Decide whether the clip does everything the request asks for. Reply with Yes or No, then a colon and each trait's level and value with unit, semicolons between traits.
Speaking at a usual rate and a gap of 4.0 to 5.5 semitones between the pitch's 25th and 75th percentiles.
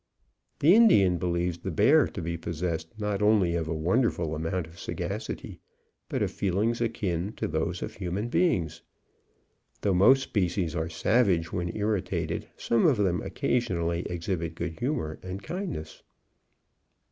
Yes: average, 145 wpm; average, 4.3 semitones